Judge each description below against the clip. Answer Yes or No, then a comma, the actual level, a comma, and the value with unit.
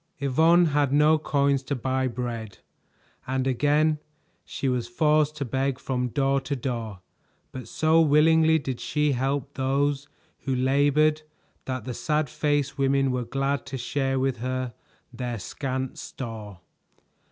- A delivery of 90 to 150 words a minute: Yes, average, 140 wpm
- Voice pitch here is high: No, low, 135 Hz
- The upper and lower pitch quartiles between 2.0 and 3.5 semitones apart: Yes, narrow, 2.4 semitones